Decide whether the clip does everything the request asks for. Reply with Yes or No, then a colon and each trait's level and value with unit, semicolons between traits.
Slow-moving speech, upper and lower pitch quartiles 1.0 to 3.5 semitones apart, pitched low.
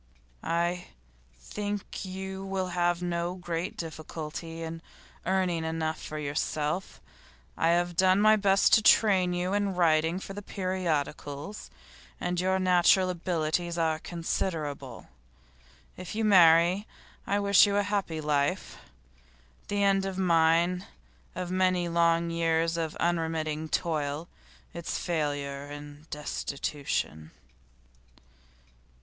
No: slow, 115 wpm; average, 2.8 semitones; medium, 170 Hz